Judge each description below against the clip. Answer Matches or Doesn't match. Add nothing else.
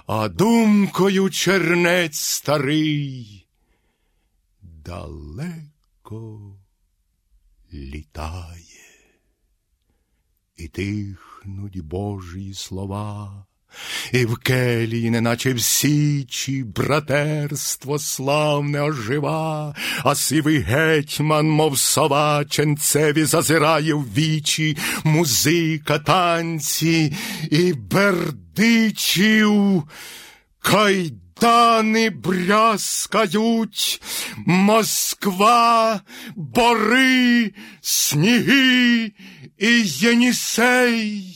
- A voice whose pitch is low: Doesn't match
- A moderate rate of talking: Doesn't match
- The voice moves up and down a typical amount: Doesn't match